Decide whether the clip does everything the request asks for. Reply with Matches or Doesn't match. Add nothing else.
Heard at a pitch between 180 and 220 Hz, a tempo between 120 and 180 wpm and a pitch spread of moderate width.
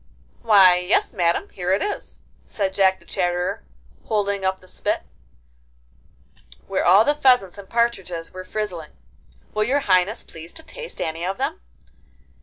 Matches